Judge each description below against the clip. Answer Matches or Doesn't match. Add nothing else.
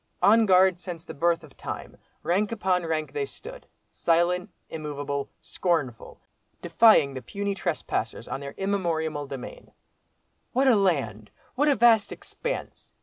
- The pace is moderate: Doesn't match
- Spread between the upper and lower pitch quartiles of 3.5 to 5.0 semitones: Doesn't match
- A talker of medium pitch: Matches